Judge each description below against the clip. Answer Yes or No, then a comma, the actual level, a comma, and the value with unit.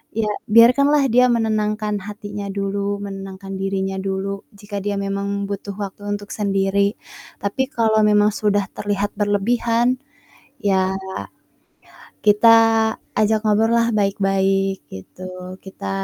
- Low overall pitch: No, high, 205 Hz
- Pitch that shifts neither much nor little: No, narrow, 1.7 semitones